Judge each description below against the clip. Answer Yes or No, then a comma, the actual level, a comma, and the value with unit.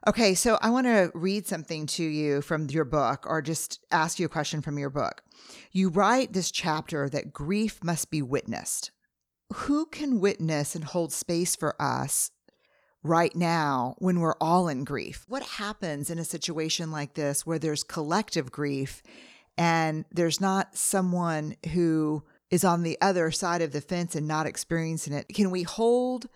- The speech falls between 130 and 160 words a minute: No, average, 175 wpm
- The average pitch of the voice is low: No, medium, 165 Hz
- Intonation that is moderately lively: Yes, average, 3.7 semitones